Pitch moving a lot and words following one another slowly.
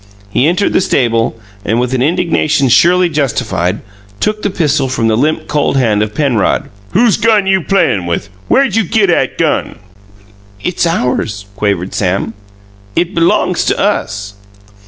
No: wide, 8.5 semitones; average, 155 wpm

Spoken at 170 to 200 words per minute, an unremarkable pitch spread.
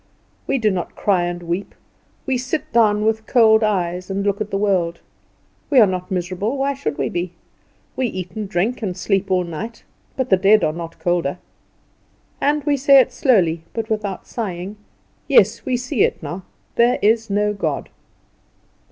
Yes: average, 180 wpm; average, 4.3 semitones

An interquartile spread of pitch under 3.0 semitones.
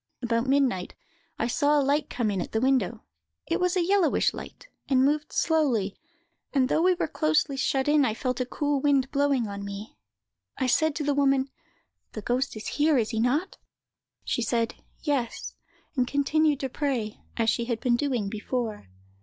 No: average, 4.0 semitones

